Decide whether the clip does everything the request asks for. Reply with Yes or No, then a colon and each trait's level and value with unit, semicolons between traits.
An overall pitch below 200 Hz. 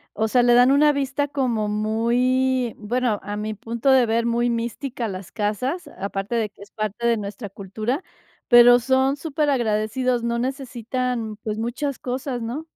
No: high, 235 Hz